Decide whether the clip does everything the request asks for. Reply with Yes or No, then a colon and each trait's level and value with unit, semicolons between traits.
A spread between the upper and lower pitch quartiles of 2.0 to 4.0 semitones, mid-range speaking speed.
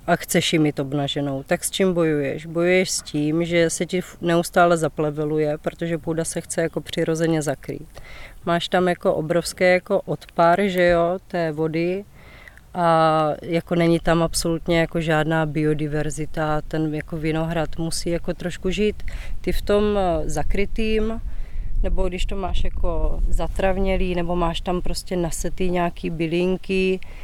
Yes: narrow, 2.3 semitones; average, 145 wpm